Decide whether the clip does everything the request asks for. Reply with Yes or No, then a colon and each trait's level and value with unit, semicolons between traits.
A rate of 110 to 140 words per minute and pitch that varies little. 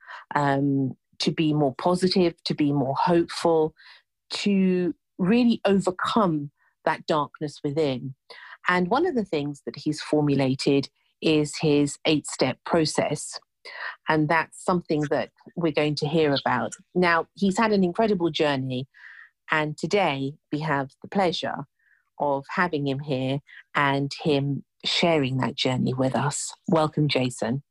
No: slow, 135 wpm; average, 4.1 semitones